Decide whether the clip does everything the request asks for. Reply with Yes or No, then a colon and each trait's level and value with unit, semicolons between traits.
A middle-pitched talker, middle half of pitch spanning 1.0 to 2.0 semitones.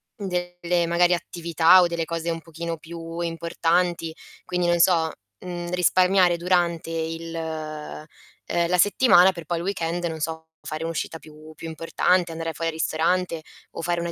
Yes: medium, 170 Hz; narrow, 1.4 semitones